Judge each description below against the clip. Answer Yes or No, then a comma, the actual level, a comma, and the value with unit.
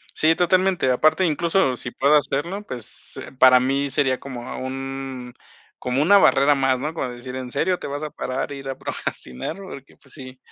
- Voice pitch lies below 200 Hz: Yes, low, 135 Hz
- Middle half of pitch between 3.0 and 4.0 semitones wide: Yes, average, 3.3 semitones